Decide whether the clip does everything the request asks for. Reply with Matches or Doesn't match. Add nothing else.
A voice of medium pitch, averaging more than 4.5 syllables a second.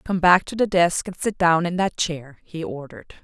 Matches